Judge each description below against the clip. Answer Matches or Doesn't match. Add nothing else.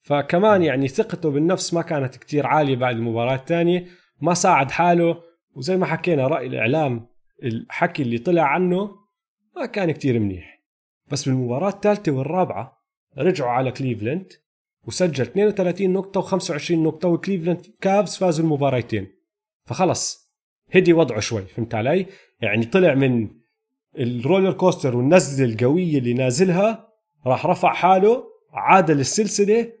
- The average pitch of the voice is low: Doesn't match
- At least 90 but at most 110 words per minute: Doesn't match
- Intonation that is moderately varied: Doesn't match